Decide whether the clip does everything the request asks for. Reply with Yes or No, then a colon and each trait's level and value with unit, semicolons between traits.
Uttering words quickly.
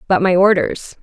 No: average, 175 wpm